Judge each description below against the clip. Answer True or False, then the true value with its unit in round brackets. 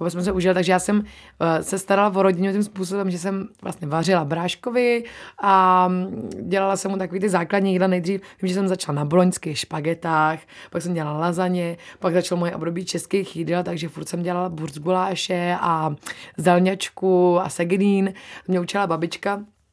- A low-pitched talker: False (185 Hz)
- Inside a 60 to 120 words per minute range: False (165 wpm)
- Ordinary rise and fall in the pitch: False (2.1 semitones)